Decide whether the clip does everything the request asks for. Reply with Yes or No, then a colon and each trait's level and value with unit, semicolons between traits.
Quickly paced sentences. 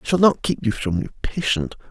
Yes: fast, 250 wpm